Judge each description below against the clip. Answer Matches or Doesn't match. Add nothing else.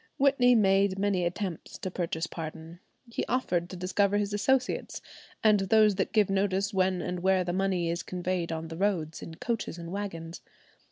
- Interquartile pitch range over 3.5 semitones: Doesn't match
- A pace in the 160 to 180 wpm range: Matches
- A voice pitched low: Doesn't match